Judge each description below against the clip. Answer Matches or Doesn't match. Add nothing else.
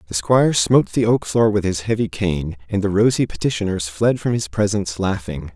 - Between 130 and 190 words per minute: Doesn't match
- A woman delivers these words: Doesn't match